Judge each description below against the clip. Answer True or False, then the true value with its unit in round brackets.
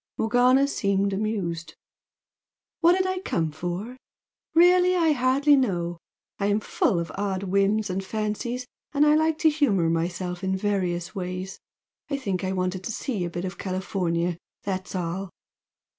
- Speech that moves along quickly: False (160 wpm)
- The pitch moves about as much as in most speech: False (5.9 semitones)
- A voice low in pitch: False (195 Hz)